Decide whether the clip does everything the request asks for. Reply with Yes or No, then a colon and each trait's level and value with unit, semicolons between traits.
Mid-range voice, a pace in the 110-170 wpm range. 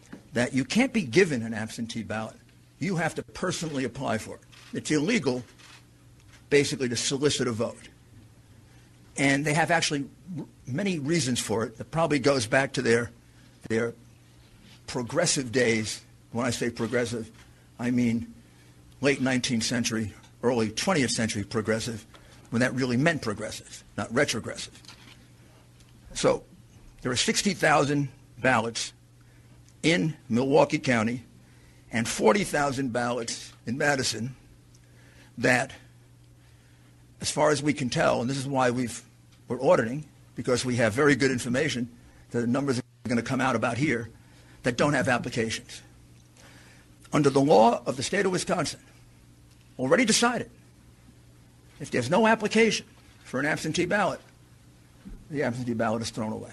No: low, 120 Hz; average, 140 wpm